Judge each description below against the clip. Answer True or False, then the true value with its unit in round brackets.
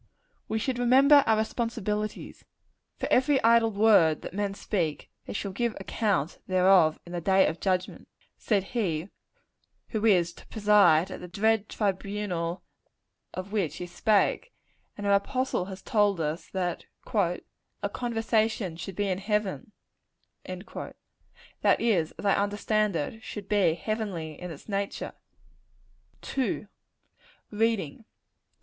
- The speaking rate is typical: False (130 wpm)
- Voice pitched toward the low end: False (200 Hz)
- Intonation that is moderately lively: True (3.5 semitones)